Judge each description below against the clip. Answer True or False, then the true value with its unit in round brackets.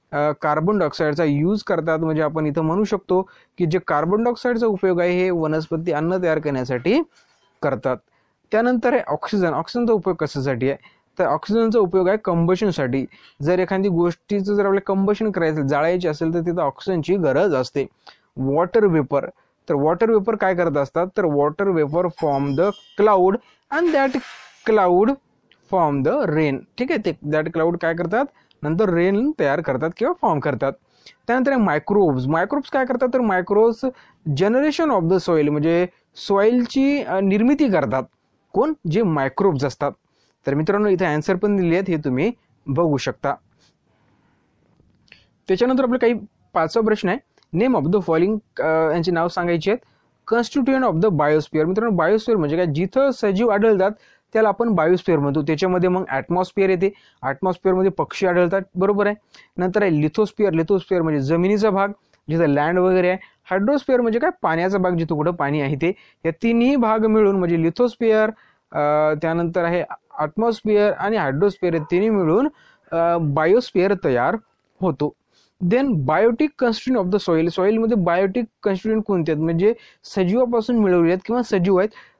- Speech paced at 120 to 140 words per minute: False (150 wpm)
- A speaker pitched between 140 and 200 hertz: True (185 Hz)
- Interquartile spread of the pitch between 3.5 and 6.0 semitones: True (4.9 semitones)